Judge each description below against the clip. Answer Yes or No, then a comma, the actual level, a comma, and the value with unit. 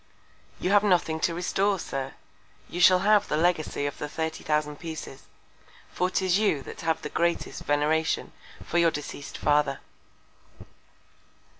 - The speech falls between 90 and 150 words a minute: Yes, average, 145 wpm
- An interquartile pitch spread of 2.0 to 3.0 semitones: No, average, 3.4 semitones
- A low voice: No, medium, 160 Hz